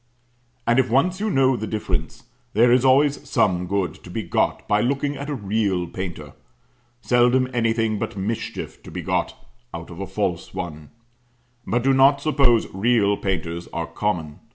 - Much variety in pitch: Yes, wide, 5.9 semitones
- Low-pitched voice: Yes, low, 110 Hz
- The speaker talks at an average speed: Yes, average, 170 wpm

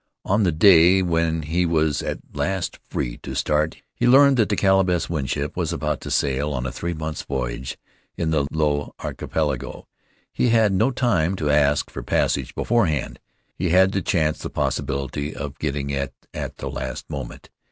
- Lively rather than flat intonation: No, average, 4.6 semitones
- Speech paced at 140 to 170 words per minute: No, average, 185 wpm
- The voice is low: Yes, very low, 80 Hz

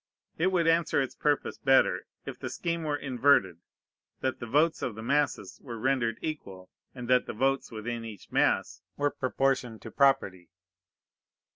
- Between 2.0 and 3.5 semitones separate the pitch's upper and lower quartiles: No, average, 4.2 semitones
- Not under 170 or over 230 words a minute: No, average, 160 wpm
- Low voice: Yes, low, 130 Hz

